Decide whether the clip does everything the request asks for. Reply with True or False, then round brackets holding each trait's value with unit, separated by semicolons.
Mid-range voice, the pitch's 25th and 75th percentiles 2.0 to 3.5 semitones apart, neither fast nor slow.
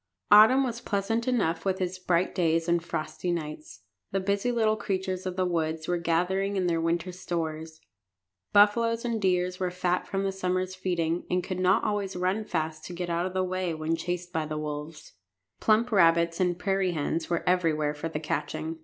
True (180 Hz; 2.7 semitones; 190 wpm)